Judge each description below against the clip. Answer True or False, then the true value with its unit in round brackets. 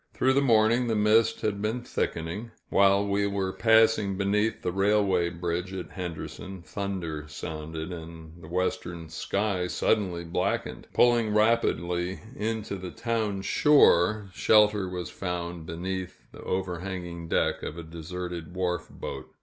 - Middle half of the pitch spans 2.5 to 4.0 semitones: True (3.6 semitones)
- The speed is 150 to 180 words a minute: False (140 wpm)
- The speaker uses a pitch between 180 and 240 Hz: False (95 Hz)